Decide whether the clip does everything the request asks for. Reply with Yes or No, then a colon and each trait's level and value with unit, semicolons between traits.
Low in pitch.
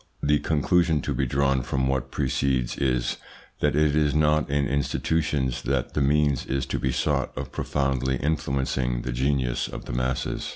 Yes: very low, 70 Hz